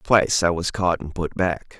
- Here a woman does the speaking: No, male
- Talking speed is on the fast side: Yes, fast, 235 wpm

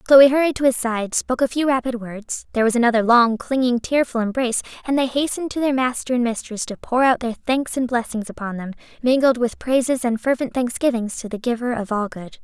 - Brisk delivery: Yes, fast, 220 wpm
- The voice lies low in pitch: No, high, 245 Hz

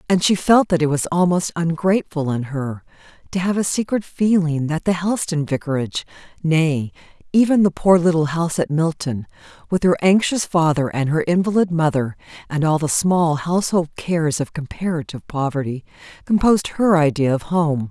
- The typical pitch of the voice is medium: Yes, medium, 165 Hz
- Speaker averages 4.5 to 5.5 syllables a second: Yes, 5.3 syllables/s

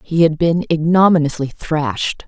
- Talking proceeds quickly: No, slow, 130 wpm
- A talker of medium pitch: Yes, medium, 160 Hz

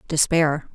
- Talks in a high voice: No, medium, 155 Hz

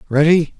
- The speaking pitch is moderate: Yes, medium, 155 Hz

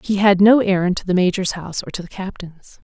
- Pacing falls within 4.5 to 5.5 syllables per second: No, 6.0 syllables/s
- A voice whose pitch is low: No, high, 190 Hz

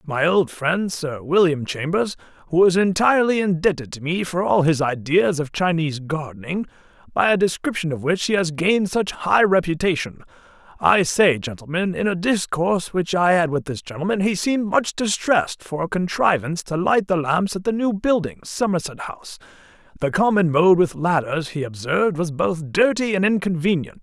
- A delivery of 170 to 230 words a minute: Yes, average, 175 wpm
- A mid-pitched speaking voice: Yes, medium, 175 Hz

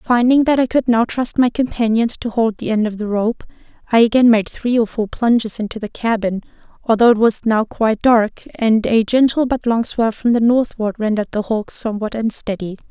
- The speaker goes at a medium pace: No, fast, 210 wpm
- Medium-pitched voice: No, high, 225 Hz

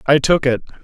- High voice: No, medium, 140 Hz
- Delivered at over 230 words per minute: No, fast, 215 wpm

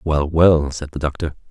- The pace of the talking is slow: No, average, 200 wpm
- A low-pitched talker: Yes, very low, 75 Hz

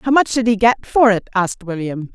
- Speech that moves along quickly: Yes, fast, 250 wpm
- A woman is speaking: Yes, female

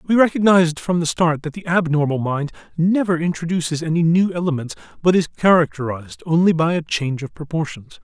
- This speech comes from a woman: No, male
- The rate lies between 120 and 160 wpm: No, average, 170 wpm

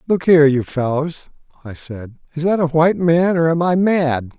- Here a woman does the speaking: No, male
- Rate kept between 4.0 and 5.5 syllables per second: Yes, 5.0 syllables/s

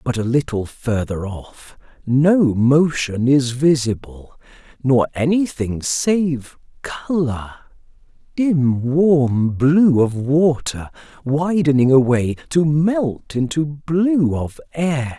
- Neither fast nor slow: No, slow, 105 wpm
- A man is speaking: Yes, male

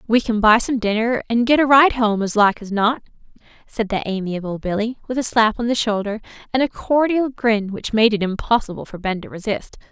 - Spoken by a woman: Yes, female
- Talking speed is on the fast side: Yes, fast, 220 wpm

